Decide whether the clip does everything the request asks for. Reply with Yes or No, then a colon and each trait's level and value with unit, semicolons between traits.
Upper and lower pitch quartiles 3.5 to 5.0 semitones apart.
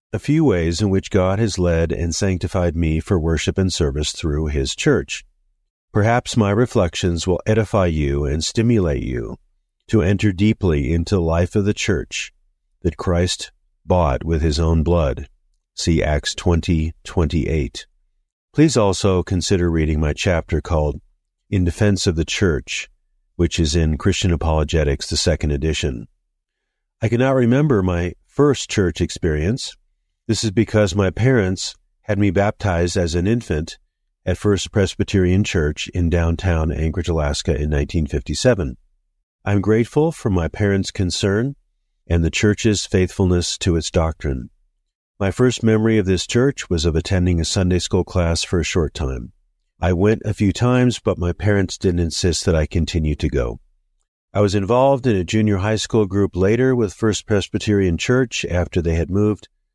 Yes: average, 4.0 semitones